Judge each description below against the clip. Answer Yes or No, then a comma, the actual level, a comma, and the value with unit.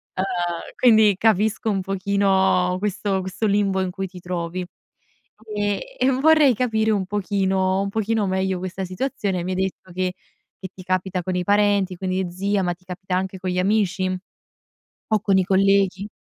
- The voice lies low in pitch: No, high, 190 Hz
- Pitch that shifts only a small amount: Yes, narrow, 1.8 semitones